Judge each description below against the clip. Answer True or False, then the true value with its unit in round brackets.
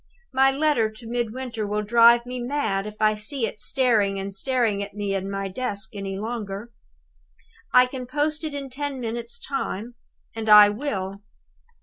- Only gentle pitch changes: False (4.0 semitones)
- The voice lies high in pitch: True (230 Hz)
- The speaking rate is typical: True (165 wpm)